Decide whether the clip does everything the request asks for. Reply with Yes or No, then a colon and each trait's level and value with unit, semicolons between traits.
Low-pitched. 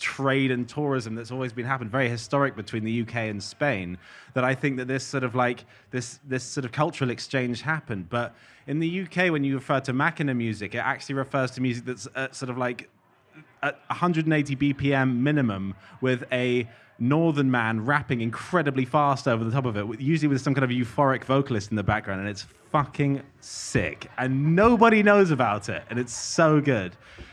Yes: low, 130 Hz